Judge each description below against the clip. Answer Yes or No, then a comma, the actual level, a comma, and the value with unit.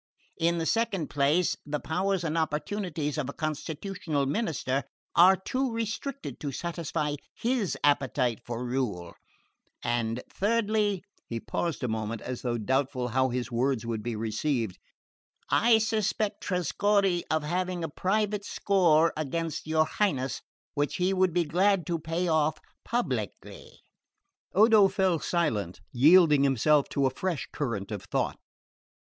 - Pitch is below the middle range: No, medium, 155 Hz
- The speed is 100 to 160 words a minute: Yes, average, 140 wpm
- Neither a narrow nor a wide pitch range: No, wide, 6.3 semitones